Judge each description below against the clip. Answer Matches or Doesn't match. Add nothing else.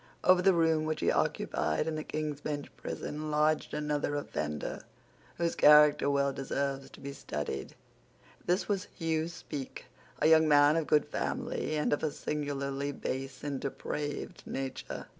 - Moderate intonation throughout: Doesn't match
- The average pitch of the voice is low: Doesn't match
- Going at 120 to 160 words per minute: Matches